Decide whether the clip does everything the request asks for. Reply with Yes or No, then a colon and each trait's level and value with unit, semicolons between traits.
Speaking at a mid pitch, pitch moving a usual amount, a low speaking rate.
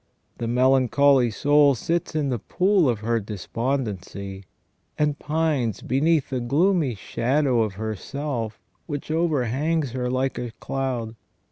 No: low, 130 Hz; average, 4.2 semitones; slow, 130 wpm